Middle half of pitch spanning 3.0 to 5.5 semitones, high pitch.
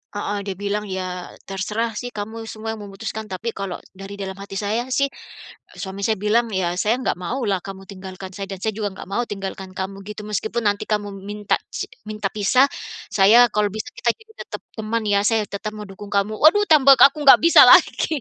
No: narrow, 2.4 semitones; high, 210 Hz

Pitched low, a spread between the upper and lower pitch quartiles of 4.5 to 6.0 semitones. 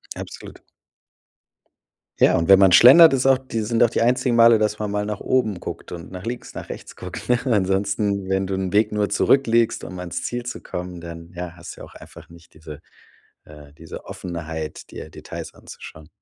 Yes: low, 100 Hz; average, 5.0 semitones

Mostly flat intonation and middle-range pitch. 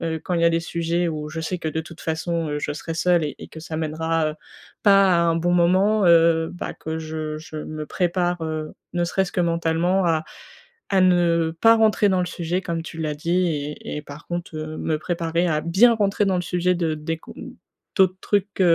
Yes: narrow, 2.1 semitones; medium, 170 Hz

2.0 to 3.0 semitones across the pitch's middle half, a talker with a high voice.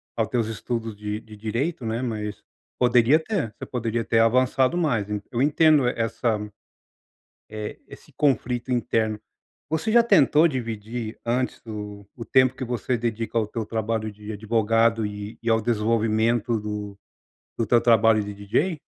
No: narrow, 2.5 semitones; low, 115 Hz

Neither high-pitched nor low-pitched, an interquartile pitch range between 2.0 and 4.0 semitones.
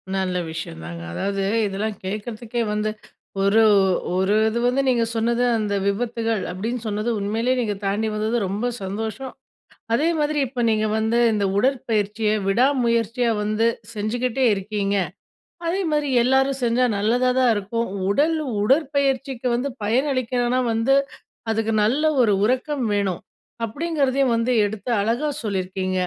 No: high, 225 Hz; average, 3.6 semitones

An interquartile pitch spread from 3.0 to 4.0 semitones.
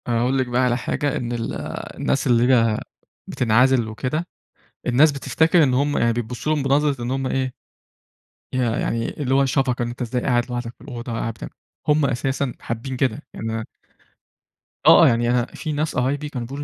No: narrow, 2.5 semitones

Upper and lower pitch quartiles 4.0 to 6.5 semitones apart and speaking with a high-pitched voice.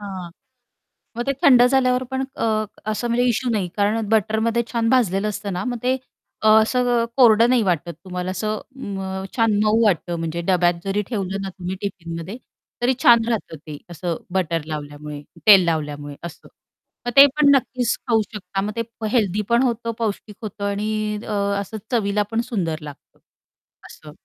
Yes: average, 4.4 semitones; high, 210 Hz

